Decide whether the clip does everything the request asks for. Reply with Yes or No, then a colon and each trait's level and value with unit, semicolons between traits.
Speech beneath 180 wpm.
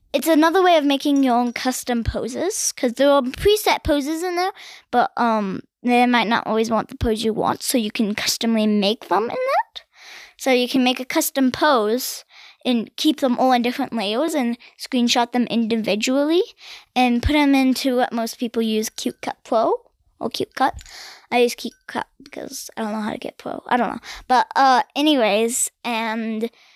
No: average, 195 wpm